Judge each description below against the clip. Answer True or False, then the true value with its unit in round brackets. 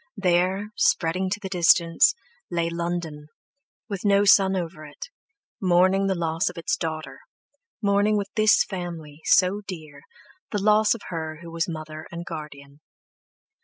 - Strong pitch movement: False (3.3 semitones)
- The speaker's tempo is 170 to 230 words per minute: False (140 wpm)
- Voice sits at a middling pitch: True (175 Hz)